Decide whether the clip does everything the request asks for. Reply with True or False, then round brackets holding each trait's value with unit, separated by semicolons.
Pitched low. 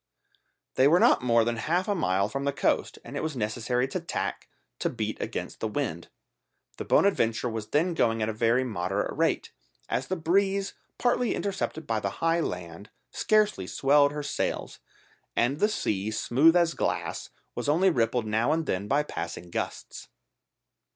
True (130 Hz)